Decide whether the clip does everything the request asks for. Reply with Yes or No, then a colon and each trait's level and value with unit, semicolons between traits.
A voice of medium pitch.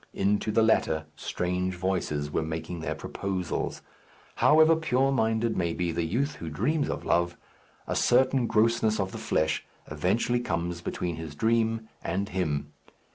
No: very low, 95 Hz